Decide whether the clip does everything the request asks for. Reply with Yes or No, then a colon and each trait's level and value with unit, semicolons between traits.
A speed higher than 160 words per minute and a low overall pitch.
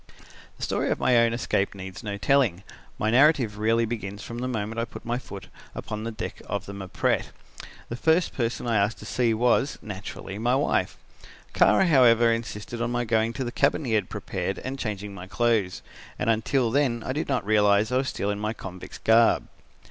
Yes: average, 200 wpm; low, 115 Hz